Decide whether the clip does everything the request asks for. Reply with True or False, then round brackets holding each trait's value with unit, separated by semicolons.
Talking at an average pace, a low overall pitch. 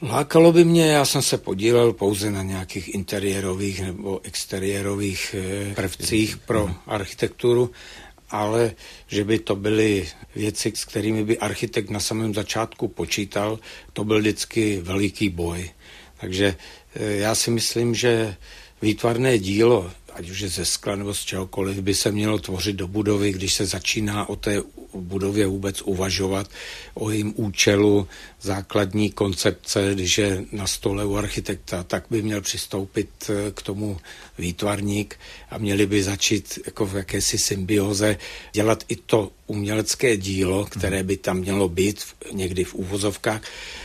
True (140 wpm; 100 Hz)